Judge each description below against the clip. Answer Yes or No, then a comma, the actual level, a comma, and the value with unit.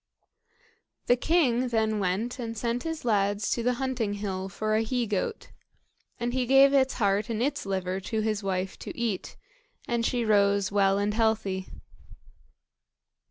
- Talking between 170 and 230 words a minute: No, average, 160 wpm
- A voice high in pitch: Yes, high, 220 Hz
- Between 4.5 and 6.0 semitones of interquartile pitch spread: No, average, 3.3 semitones